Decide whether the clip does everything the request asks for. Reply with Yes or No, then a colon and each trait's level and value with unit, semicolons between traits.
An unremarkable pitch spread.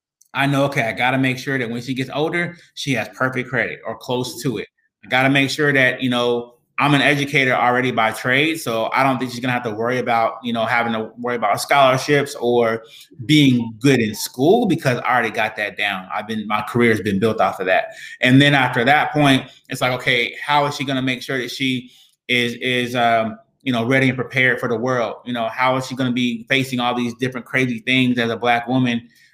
No: narrow, 2.1 semitones